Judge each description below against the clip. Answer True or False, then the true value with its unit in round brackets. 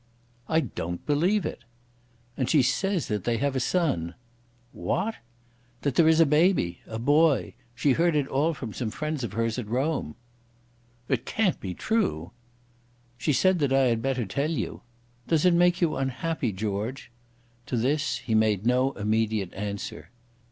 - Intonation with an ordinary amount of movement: False (6.3 semitones)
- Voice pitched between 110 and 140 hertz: True (135 Hz)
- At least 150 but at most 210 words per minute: True (165 wpm)